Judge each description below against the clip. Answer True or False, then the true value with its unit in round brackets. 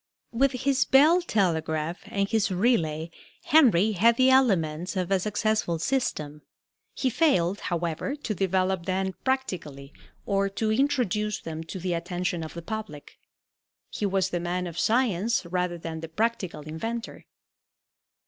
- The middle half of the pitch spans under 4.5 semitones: False (5.3 semitones)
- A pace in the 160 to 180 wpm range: False (140 wpm)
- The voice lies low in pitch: False (190 Hz)